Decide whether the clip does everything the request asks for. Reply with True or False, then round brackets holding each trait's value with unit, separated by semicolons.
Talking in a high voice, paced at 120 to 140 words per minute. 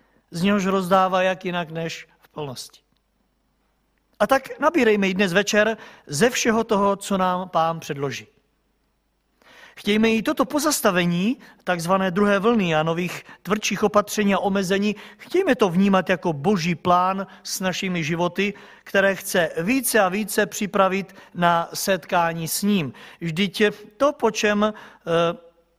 True (195 Hz; 135 wpm)